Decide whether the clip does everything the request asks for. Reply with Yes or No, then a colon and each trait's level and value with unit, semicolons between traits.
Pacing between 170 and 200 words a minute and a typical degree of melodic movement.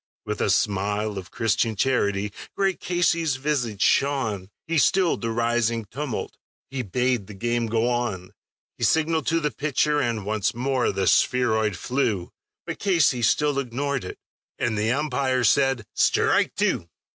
No: average, 150 wpm; average, 4.8 semitones